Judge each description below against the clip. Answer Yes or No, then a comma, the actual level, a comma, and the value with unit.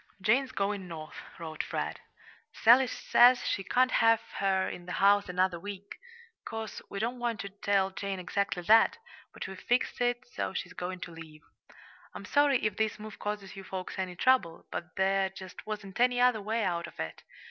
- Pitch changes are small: No, average, 3.5 semitones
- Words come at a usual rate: Yes, average, 185 wpm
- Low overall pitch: No, high, 200 Hz